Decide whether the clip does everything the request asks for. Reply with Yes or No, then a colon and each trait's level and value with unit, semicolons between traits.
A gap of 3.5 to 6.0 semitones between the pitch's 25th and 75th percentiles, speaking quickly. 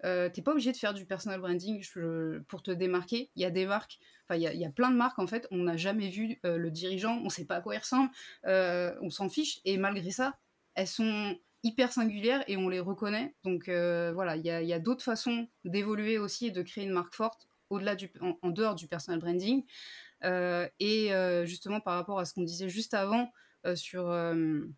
Yes: average, 3.9 semitones; fast, 235 wpm